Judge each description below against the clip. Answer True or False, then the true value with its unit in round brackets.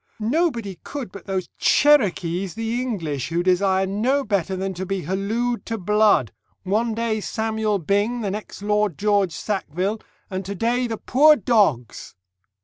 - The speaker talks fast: False (150 wpm)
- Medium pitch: False (205 Hz)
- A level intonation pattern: False (3.3 semitones)